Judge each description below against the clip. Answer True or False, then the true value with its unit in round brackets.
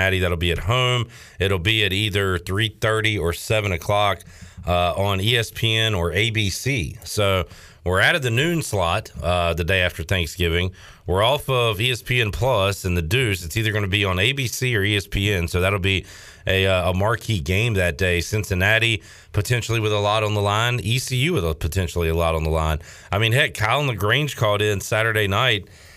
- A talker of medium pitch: False (100 Hz)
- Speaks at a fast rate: False (190 wpm)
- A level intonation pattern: False (3.6 semitones)